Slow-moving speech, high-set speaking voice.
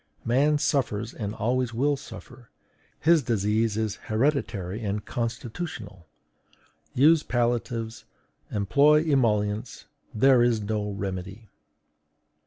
No: slow, 95 wpm; low, 115 Hz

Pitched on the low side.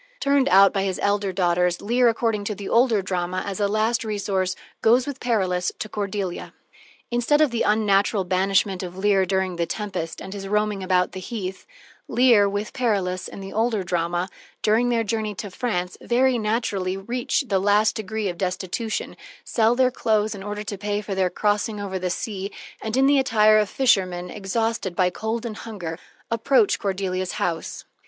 No: high, 205 Hz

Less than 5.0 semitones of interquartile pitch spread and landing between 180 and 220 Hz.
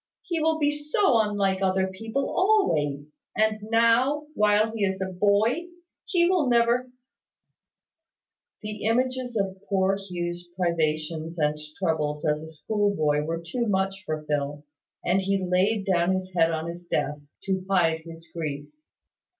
No: wide, 5.5 semitones; high, 190 Hz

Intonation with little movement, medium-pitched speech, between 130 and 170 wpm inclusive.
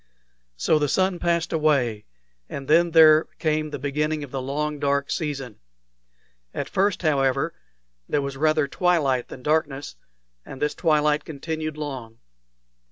Yes: narrow, 2.3 semitones; medium, 150 Hz; average, 140 wpm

